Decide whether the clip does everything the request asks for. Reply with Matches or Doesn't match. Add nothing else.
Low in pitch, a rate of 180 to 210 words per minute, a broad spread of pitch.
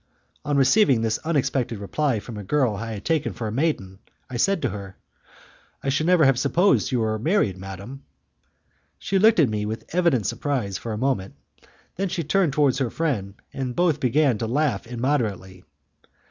Matches